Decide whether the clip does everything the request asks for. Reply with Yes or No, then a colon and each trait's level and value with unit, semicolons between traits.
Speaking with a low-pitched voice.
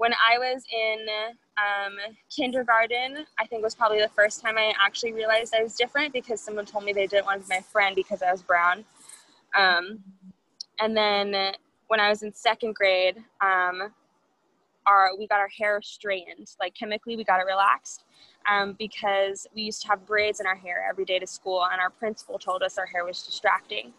No: high, 210 Hz